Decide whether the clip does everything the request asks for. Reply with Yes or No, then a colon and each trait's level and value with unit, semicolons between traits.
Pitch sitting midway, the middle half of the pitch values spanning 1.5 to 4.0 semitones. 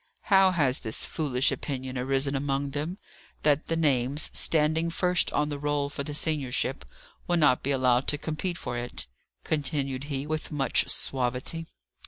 Yes: medium, 145 Hz; average, 2.9 semitones